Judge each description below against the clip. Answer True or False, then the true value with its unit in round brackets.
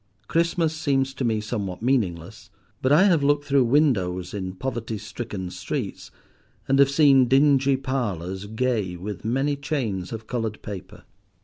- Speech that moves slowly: False (145 wpm)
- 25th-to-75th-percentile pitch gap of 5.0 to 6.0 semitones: True (5.6 semitones)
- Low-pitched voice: True (120 Hz)